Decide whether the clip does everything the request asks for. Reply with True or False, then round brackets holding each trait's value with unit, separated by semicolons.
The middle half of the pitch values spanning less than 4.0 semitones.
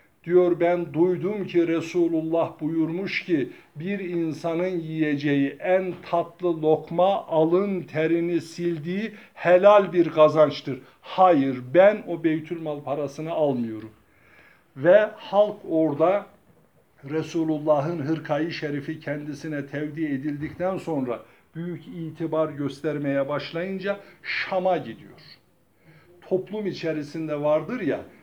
True (2.8 semitones)